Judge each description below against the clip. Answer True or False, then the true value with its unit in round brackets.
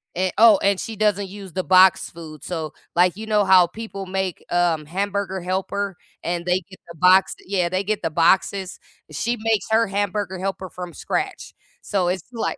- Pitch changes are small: True (2.1 semitones)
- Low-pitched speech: False (190 Hz)